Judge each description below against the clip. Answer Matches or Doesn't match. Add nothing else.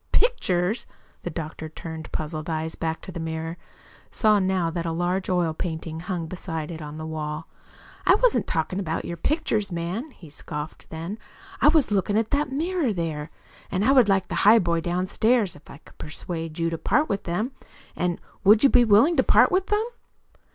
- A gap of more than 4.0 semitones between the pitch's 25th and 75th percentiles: Matches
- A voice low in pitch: Doesn't match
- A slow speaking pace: Doesn't match